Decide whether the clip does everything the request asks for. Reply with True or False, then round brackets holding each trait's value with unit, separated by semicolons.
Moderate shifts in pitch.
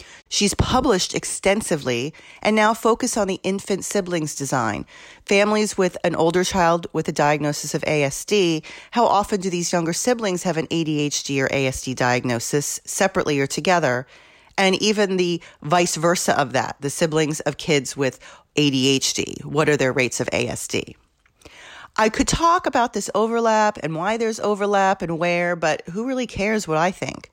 False (5.7 semitones)